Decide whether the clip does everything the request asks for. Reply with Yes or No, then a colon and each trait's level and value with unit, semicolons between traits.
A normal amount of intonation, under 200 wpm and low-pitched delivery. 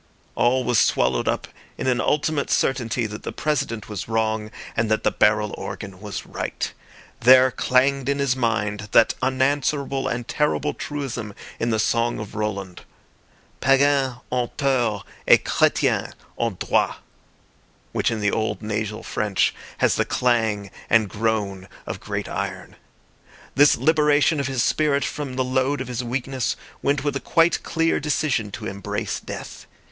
Yes: average, 4.4 semitones; average, 150 wpm; low, 120 Hz